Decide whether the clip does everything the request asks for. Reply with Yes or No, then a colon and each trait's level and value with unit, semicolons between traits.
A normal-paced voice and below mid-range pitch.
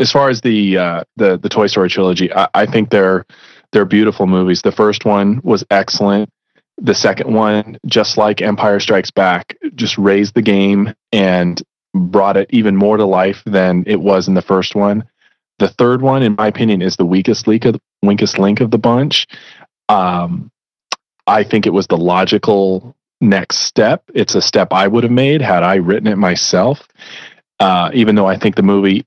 Yes: average, 190 wpm; low, 100 Hz